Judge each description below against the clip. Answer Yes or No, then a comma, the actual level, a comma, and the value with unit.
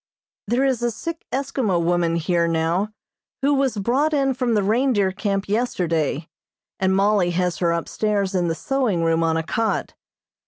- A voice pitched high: Yes, high, 200 Hz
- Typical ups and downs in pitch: No, wide, 6.3 semitones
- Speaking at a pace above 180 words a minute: No, average, 165 wpm